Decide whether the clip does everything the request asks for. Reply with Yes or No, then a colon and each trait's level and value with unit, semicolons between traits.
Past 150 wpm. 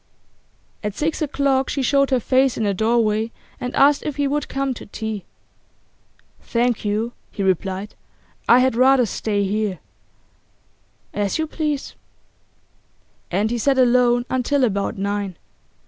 No: average, 140 wpm